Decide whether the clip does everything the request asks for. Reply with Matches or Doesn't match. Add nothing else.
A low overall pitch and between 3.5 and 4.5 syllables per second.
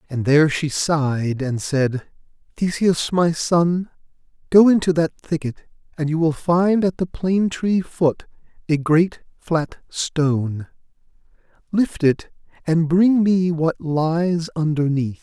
Doesn't match